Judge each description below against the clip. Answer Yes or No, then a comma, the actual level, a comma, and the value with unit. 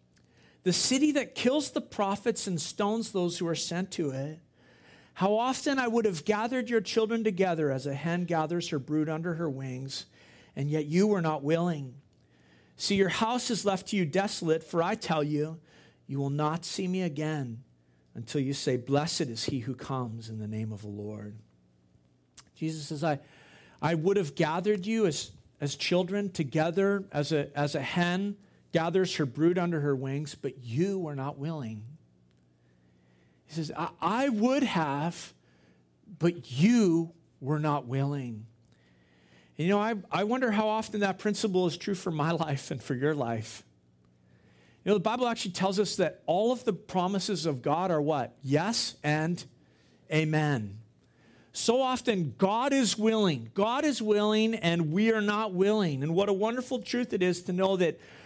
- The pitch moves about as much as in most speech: No, wide, 6.5 semitones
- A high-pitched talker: No, medium, 165 Hz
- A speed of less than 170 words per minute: No, average, 175 wpm